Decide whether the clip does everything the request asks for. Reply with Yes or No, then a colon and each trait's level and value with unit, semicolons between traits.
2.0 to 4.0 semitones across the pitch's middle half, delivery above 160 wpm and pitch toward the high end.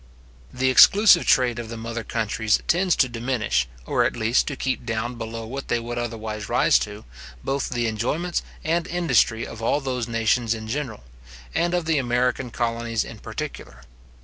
No: average, 2.9 semitones; average, 175 wpm; low, 120 Hz